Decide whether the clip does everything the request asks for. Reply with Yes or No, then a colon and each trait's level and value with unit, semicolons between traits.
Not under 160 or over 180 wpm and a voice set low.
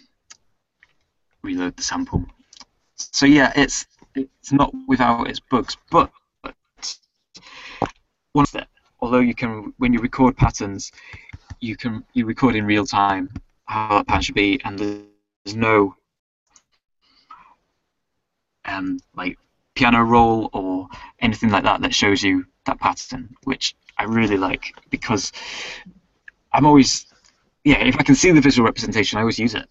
No: average, 140 wpm; low, 120 Hz